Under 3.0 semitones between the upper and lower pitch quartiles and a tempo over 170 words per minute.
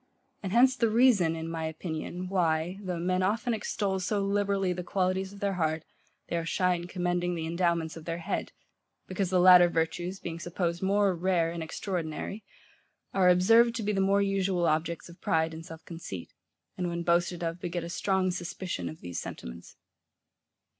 Yes: narrow, 2.6 semitones; average, 180 wpm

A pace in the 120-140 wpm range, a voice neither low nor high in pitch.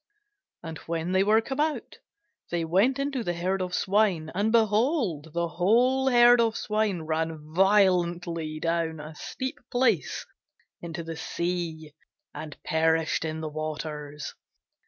Yes: slow, 135 wpm; medium, 175 Hz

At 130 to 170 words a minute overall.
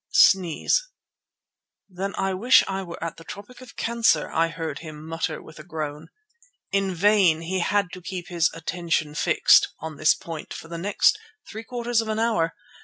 No: average, 180 wpm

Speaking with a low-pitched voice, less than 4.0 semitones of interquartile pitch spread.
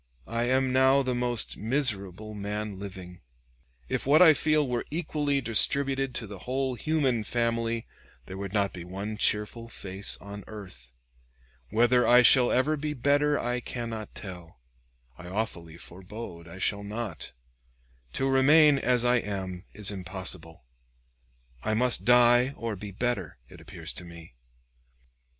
No: low, 115 Hz; average, 4.8 semitones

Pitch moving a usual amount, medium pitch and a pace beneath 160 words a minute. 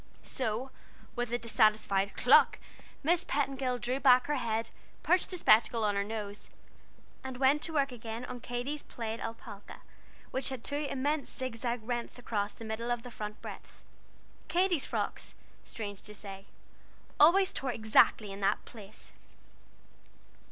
No: average, 3.6 semitones; high, 240 Hz; average, 145 wpm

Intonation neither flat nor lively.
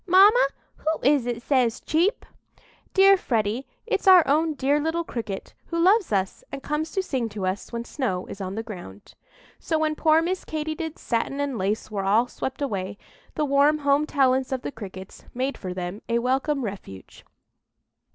No: wide, 6.5 semitones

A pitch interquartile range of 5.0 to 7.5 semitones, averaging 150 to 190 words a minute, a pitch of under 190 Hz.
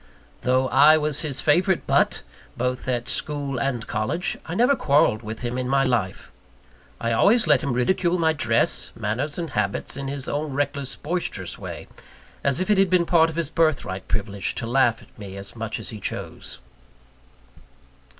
Yes: average, 5.3 semitones; average, 180 wpm; low, 135 Hz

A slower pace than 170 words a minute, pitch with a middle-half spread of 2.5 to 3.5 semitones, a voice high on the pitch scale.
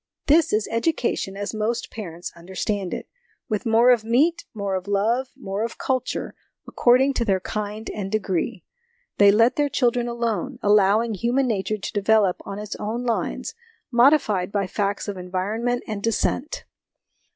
Yes: average, 155 wpm; average, 3.2 semitones; high, 215 Hz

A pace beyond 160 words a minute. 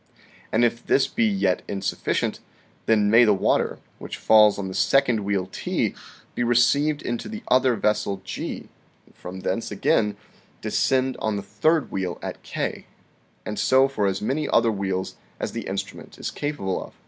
Yes: average, 170 wpm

